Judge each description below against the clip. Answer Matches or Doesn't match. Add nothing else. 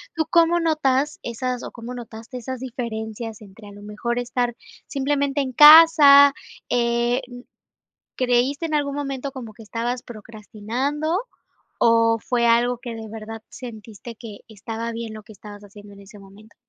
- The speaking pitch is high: Matches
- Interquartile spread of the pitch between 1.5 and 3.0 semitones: Doesn't match